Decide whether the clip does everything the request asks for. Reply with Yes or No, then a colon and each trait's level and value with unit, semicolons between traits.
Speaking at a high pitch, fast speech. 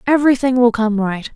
No: high, 240 Hz; average, 175 wpm